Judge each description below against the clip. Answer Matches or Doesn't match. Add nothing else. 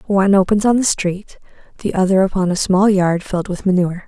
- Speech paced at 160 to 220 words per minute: Matches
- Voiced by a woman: Matches